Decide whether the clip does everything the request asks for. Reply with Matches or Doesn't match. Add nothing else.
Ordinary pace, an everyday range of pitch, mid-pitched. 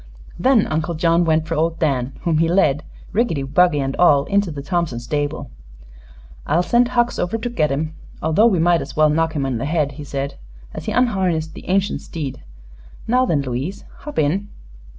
Matches